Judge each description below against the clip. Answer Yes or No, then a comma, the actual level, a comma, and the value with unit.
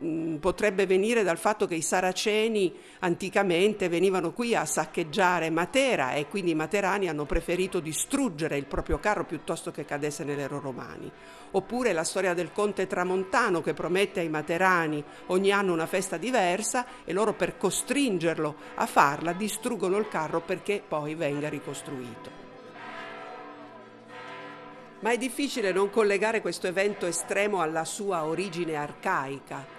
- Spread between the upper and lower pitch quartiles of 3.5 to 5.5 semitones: Yes, average, 4.0 semitones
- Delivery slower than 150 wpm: Yes, average, 140 wpm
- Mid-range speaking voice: Yes, medium, 180 Hz